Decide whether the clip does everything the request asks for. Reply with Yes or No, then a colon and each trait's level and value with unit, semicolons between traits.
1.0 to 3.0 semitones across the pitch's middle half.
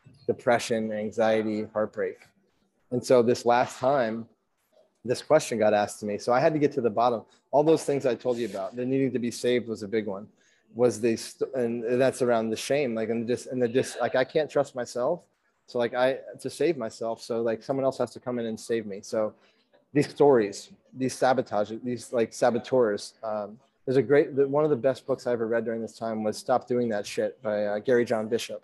Yes: narrow, 2.6 semitones